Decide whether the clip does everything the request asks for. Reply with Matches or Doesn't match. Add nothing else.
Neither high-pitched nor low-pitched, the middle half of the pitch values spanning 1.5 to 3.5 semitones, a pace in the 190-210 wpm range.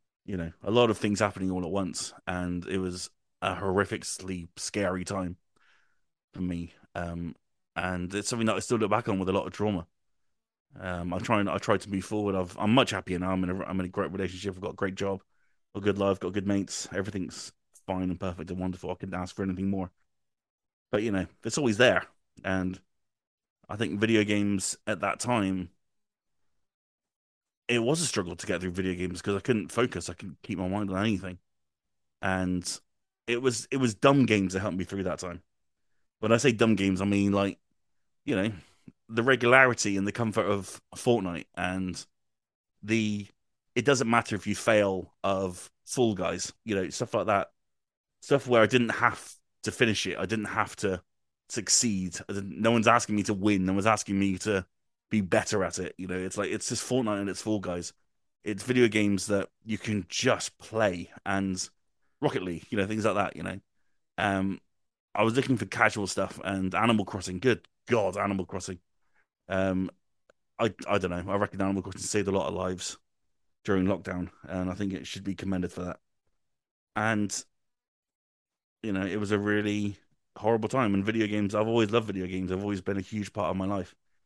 Doesn't match